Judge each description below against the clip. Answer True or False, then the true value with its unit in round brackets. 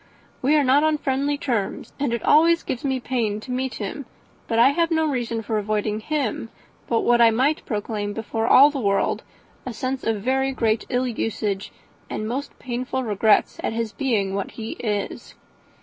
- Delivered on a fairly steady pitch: False (3.7 semitones)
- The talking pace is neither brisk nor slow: True (185 wpm)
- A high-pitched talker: True (240 Hz)